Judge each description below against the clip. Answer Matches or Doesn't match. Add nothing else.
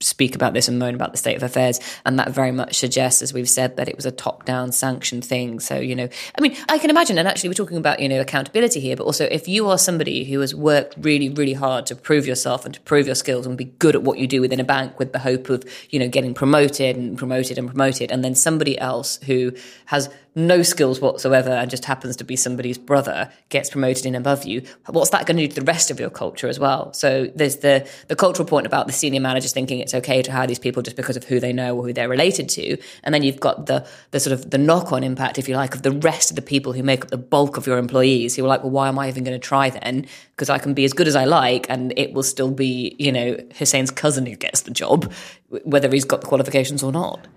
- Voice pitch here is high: Doesn't match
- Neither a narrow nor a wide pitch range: Doesn't match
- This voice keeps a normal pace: Doesn't match